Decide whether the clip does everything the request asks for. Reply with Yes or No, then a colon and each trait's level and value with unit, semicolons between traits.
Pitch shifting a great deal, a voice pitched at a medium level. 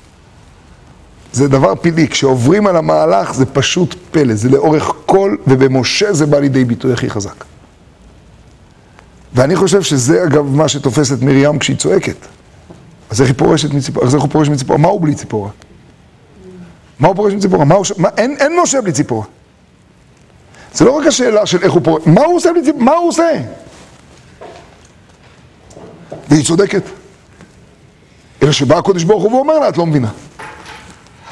Yes: wide, 6.2 semitones; medium, 150 Hz